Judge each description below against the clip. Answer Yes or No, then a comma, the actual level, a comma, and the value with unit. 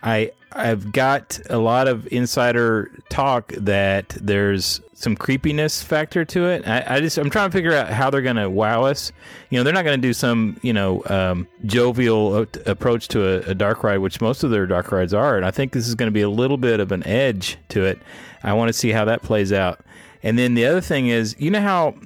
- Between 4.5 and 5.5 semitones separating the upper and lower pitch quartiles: Yes, average, 4.8 semitones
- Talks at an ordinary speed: No, fast, 235 wpm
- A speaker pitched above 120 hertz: No, low, 115 Hz